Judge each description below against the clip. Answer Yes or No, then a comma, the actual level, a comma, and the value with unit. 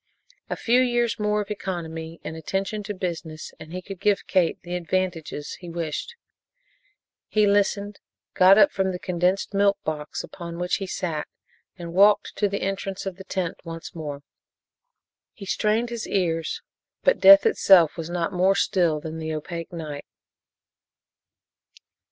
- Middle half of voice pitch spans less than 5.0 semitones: Yes, average, 3.3 semitones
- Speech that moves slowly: No, average, 155 wpm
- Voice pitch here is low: No, medium, 185 Hz